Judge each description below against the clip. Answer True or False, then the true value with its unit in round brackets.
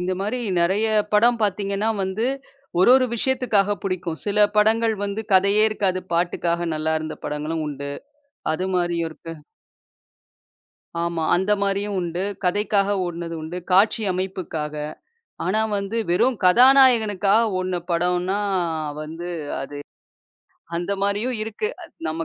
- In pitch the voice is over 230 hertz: False (190 Hz)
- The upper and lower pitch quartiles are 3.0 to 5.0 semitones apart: True (3.6 semitones)